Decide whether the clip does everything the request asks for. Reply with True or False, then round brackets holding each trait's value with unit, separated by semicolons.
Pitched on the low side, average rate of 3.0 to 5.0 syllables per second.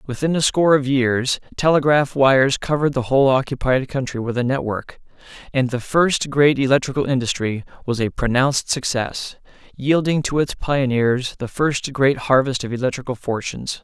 False (130 Hz; 5.2 syllables/s)